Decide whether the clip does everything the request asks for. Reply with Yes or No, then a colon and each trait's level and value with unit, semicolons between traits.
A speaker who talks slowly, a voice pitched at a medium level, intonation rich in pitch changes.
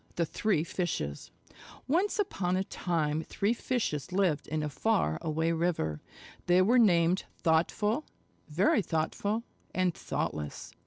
No: slow, 125 wpm; medium, 175 Hz; average, 4.8 semitones